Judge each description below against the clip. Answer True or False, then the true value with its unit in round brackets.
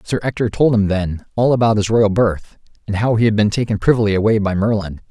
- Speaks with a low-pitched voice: True (105 Hz)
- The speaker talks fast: True (235 wpm)